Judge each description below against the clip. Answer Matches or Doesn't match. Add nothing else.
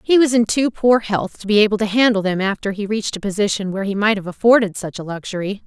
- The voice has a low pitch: Doesn't match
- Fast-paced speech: Matches